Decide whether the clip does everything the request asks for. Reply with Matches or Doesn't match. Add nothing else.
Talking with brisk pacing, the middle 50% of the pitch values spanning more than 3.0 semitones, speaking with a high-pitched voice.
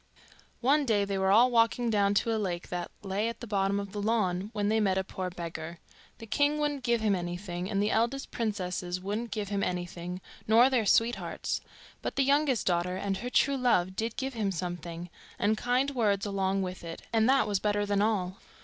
Matches